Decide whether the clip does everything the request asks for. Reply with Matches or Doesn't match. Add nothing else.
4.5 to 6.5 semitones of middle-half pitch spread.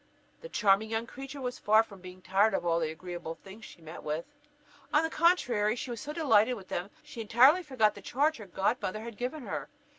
Matches